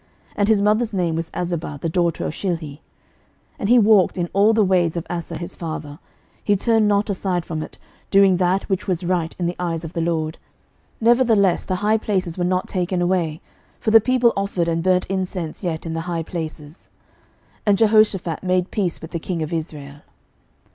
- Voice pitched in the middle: Yes, medium, 180 Hz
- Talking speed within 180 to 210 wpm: Yes, average, 200 wpm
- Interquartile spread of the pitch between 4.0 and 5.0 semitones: No, average, 3.3 semitones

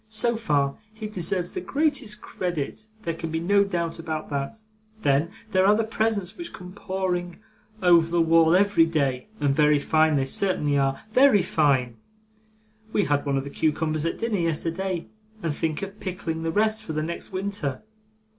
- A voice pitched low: No, medium, 170 Hz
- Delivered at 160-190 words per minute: Yes, average, 175 wpm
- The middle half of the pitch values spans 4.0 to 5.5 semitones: Yes, average, 4.8 semitones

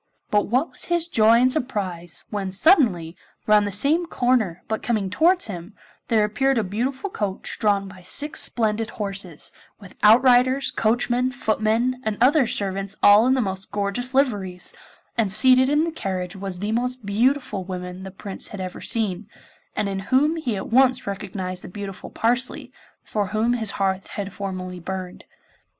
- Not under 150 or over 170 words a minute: Yes, average, 165 wpm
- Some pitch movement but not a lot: Yes, average, 4.6 semitones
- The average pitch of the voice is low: No, high, 210 Hz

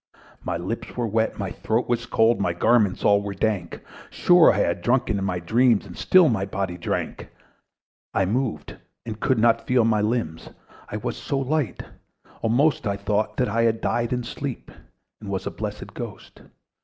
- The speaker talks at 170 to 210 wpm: Yes, average, 180 wpm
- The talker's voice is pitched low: Yes, low, 110 Hz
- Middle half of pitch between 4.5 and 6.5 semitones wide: No, average, 3.6 semitones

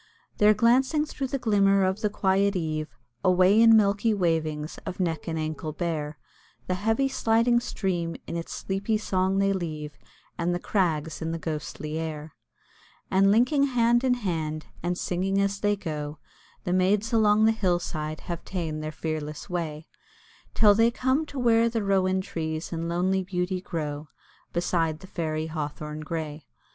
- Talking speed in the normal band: Yes, average, 165 wpm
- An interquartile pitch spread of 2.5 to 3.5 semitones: No, average, 4.8 semitones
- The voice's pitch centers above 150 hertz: Yes, medium, 185 Hz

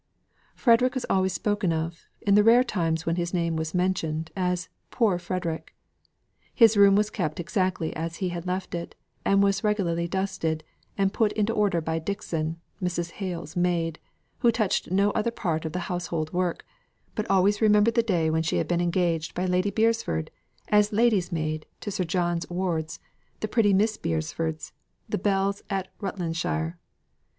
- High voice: No, medium, 180 Hz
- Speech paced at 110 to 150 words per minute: No, average, 170 wpm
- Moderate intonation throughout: Yes, average, 3.7 semitones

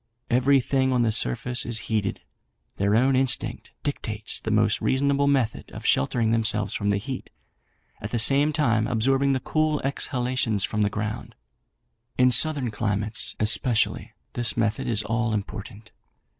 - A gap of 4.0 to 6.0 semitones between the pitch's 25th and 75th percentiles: No, average, 3.6 semitones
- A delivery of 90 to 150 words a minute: Yes, average, 145 wpm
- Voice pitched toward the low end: Yes, low, 115 Hz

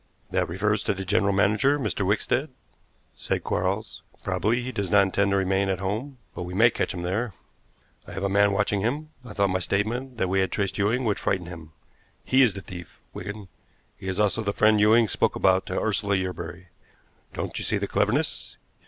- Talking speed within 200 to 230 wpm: Yes, fast, 205 wpm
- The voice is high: No, low, 100 Hz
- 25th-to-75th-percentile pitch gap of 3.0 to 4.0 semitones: No, narrow, 2.4 semitones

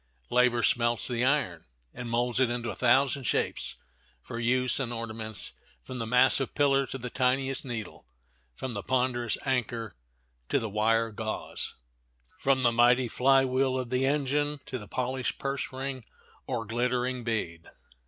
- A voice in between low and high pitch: No, low, 125 Hz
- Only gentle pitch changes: Yes, narrow, 2.1 semitones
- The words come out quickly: No, average, 155 wpm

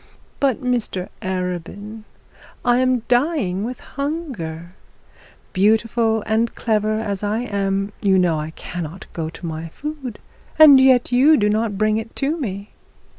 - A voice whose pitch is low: No, high, 215 Hz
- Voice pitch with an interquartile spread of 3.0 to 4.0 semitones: No, average, 4.8 semitones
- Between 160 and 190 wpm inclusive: No, average, 140 wpm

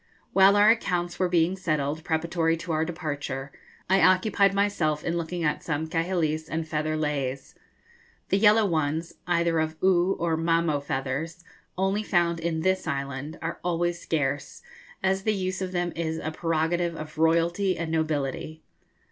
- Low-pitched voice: No, medium, 165 Hz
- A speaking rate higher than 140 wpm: Yes, average, 155 wpm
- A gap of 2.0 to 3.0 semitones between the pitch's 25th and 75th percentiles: Yes, narrow, 2.4 semitones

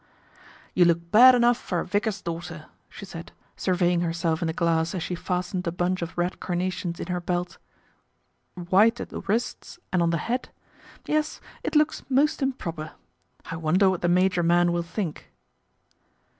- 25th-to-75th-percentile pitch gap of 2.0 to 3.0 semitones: Yes, narrow, 2.6 semitones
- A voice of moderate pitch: Yes, medium, 175 Hz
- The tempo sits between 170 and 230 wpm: Yes, average, 180 wpm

